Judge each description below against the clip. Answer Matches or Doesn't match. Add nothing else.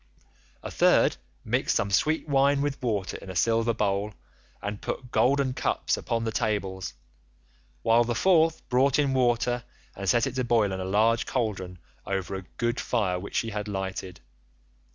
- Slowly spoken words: Doesn't match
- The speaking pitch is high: Doesn't match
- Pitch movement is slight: Doesn't match